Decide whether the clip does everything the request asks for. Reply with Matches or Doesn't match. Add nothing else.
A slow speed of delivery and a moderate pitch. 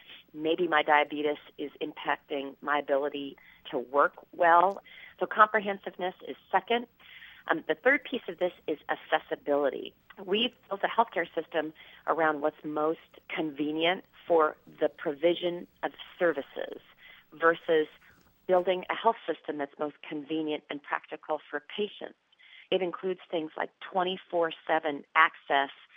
Matches